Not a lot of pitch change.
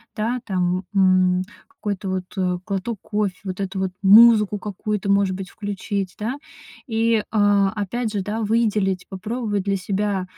Yes: narrow, 2.1 semitones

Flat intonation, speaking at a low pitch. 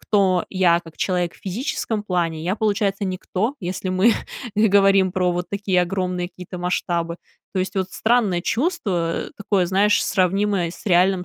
No: narrow, 2.3 semitones; medium, 185 Hz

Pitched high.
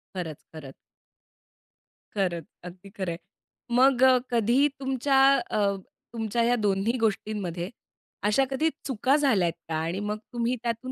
Yes: high, 215 Hz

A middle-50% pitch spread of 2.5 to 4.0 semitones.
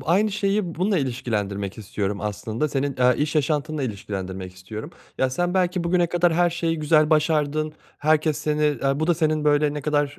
No: average, 4.7 semitones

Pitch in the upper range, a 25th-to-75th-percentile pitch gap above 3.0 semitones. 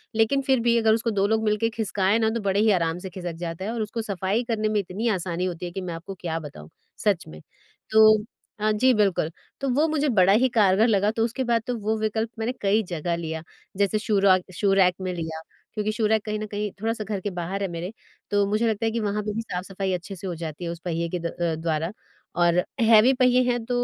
Yes: high, 205 Hz; average, 3.7 semitones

